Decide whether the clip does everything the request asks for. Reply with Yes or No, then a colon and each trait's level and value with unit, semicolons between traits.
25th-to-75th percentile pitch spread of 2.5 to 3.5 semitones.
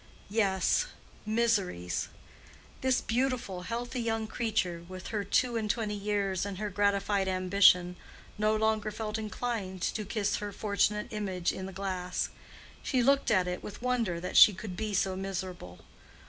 Yes: average, 2.9 semitones